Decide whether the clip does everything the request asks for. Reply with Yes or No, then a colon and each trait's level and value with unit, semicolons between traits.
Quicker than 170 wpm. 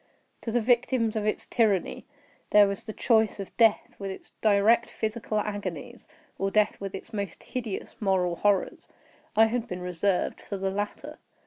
No: average, 165 wpm